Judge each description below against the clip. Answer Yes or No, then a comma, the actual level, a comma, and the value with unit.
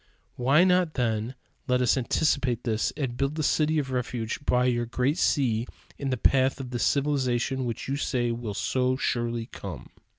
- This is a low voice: Yes, low, 125 Hz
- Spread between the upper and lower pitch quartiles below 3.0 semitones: Yes, narrow, 2.5 semitones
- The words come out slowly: No, average, 175 wpm